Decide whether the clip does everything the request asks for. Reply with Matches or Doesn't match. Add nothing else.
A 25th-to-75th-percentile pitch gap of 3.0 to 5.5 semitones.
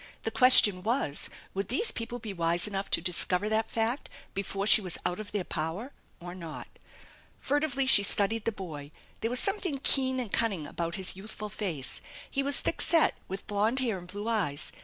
Matches